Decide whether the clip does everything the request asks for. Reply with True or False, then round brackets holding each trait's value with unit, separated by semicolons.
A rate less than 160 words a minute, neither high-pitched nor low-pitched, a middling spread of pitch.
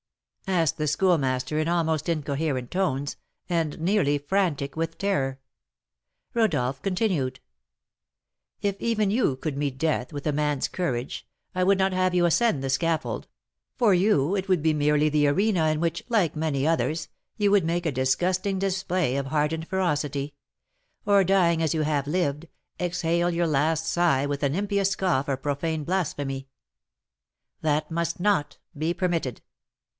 True (150 wpm; 160 Hz; 4.3 semitones)